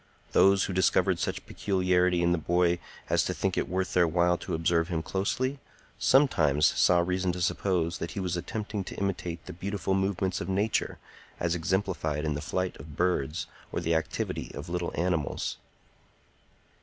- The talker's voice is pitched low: Yes, very low, 90 Hz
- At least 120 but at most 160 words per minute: No, average, 170 wpm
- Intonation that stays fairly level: Yes, narrow, 2.3 semitones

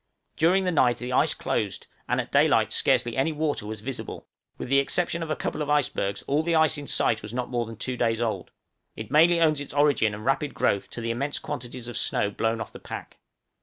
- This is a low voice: Yes, low, 130 Hz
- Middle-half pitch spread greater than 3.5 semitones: Yes, average, 4.7 semitones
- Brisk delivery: Yes, fast, 230 wpm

